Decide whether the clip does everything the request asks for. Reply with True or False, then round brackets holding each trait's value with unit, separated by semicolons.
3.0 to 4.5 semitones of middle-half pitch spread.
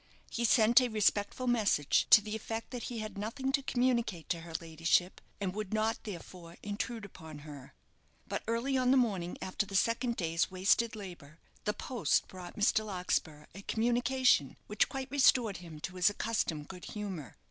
False (4.9 semitones)